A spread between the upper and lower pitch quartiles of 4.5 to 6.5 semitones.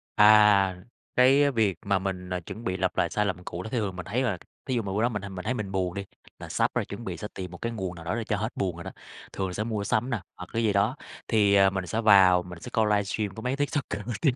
No: average, 3.3 semitones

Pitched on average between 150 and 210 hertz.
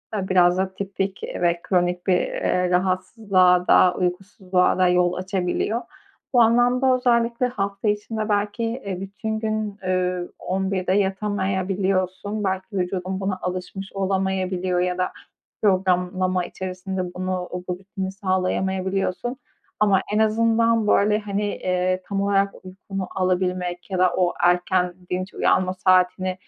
Yes: high, 190 Hz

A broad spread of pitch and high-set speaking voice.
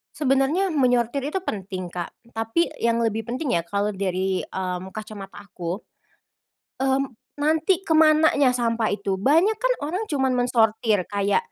Yes: wide, 6.7 semitones; high, 235 Hz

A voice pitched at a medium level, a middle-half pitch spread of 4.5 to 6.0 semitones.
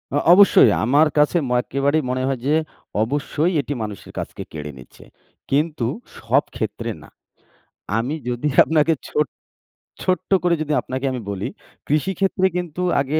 No: medium, 145 Hz; average, 3.7 semitones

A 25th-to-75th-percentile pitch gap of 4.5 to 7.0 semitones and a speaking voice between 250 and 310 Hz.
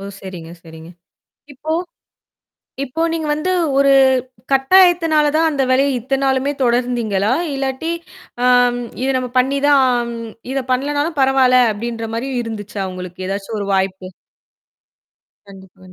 Yes: average, 5.2 semitones; very high, 255 Hz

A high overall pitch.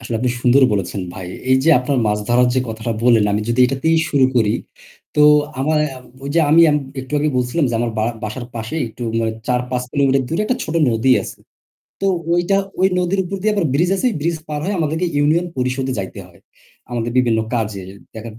No: low, 130 Hz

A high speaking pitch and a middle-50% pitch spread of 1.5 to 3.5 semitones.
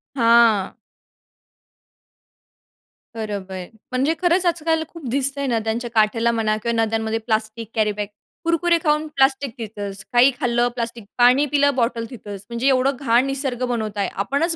No: high, 240 Hz; average, 3.9 semitones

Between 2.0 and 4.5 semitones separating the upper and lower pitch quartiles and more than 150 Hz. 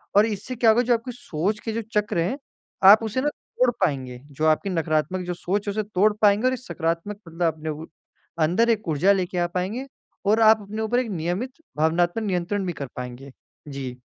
No: average, 5.2 semitones; high, 190 Hz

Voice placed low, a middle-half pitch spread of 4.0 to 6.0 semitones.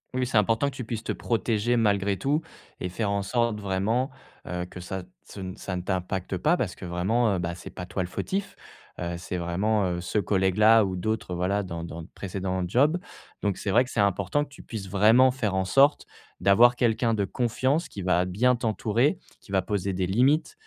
Yes: low, 100 Hz; average, 4.3 semitones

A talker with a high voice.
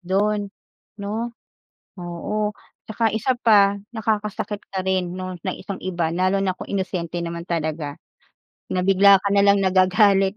Yes: high, 195 Hz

